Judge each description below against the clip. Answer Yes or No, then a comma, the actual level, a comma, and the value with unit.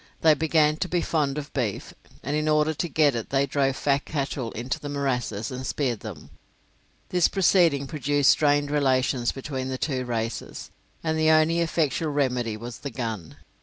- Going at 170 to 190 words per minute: Yes, average, 175 wpm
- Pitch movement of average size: Yes, average, 3.2 semitones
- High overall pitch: No, medium, 140 Hz